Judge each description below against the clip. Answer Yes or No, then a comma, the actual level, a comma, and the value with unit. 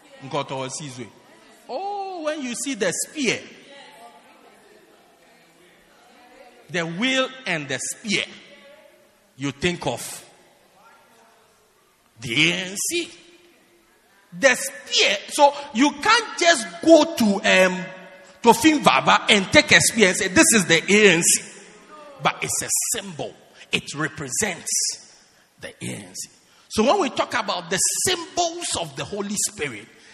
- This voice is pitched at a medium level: No, high, 215 Hz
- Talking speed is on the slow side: Yes, slow, 110 wpm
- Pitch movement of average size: No, wide, 8.5 semitones